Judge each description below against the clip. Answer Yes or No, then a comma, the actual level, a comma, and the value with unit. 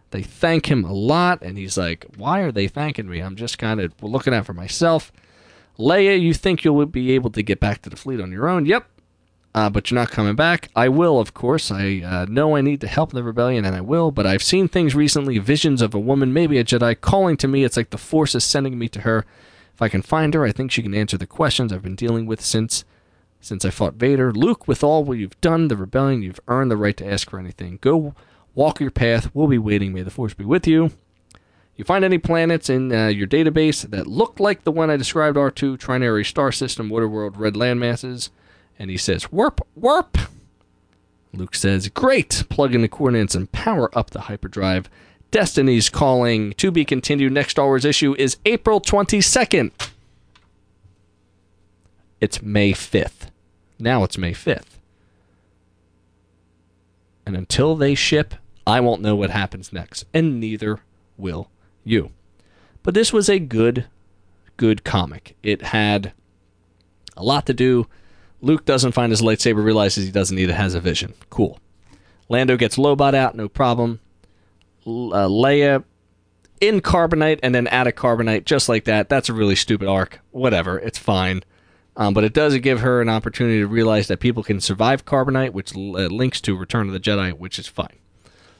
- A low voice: Yes, low, 110 Hz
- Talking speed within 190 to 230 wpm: Yes, average, 195 wpm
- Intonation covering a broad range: Yes, wide, 5.8 semitones